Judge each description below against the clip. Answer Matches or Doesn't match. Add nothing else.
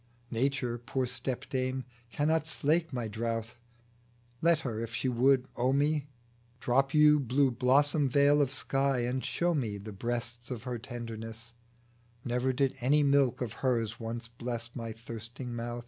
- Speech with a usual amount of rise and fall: Matches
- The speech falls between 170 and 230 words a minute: Doesn't match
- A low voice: Matches